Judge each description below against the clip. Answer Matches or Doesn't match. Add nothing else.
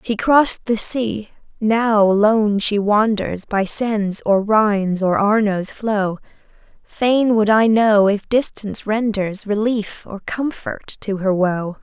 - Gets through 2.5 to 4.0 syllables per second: Matches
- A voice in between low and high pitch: Doesn't match